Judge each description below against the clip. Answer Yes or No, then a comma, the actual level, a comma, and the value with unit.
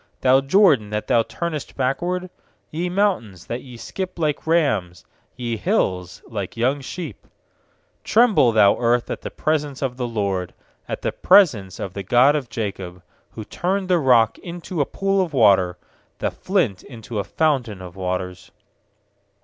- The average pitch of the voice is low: Yes, low, 125 Hz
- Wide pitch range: Yes, wide, 8.6 semitones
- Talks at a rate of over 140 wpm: Yes, average, 160 wpm